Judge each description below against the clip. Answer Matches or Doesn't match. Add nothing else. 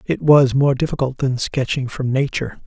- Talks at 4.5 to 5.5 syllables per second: Matches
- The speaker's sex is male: Matches